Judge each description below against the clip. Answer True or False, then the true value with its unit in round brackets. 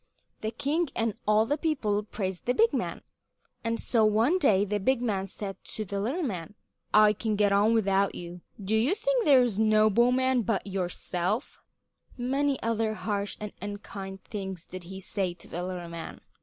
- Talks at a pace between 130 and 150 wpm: False (180 wpm)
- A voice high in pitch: True (215 Hz)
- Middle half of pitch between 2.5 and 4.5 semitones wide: True (3.8 semitones)